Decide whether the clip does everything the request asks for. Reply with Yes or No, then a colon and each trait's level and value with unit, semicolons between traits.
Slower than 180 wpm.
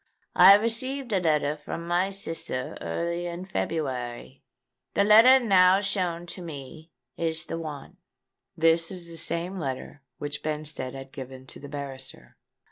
Yes: average, 140 wpm